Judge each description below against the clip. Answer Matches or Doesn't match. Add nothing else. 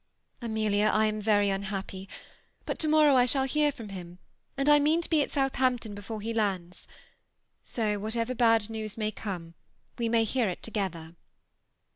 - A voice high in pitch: Matches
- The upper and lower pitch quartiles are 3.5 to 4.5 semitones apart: Matches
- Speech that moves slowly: Doesn't match